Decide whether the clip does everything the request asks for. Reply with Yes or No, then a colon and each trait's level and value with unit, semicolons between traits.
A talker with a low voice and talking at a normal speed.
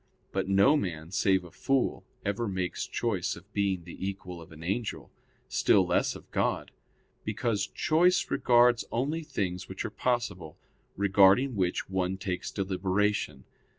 Yes: low, 100 Hz; average, 145 wpm